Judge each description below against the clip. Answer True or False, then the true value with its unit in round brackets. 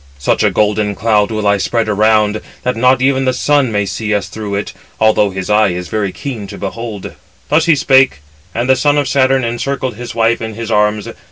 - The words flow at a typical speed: False (215 wpm)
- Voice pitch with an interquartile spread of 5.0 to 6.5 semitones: False (3.6 semitones)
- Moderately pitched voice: False (110 Hz)